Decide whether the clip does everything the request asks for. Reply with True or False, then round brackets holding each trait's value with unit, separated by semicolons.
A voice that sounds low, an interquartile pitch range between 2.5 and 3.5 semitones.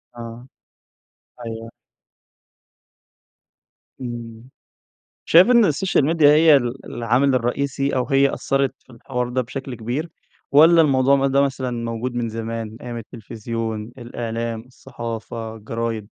True (120 Hz; 3.0 semitones)